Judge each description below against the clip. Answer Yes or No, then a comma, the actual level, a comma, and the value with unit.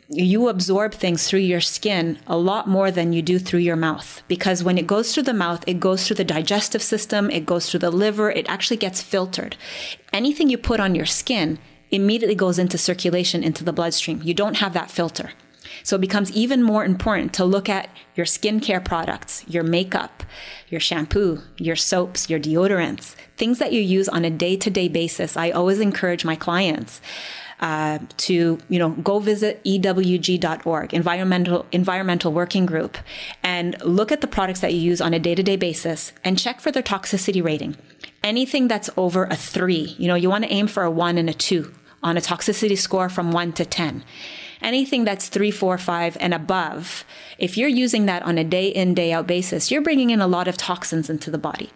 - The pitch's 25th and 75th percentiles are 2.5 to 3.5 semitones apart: Yes, average, 3.2 semitones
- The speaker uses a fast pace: No, average, 195 wpm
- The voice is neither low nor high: Yes, medium, 180 Hz